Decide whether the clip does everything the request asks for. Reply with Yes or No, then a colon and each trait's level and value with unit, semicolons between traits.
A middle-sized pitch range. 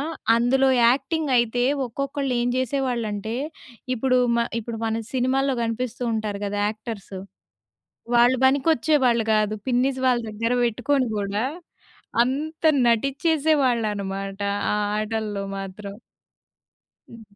Yes: average, 3.7 semitones